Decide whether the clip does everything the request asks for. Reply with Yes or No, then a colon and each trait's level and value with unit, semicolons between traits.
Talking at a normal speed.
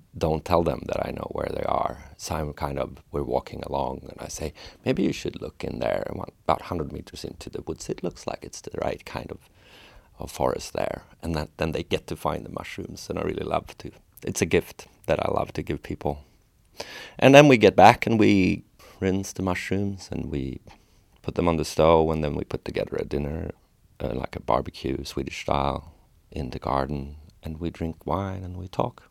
No: fast, 220 wpm